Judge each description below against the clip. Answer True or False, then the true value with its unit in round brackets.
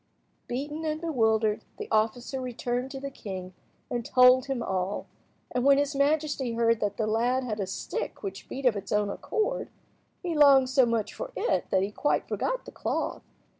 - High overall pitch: True (250 Hz)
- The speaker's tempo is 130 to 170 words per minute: False (185 wpm)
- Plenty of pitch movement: False (4.4 semitones)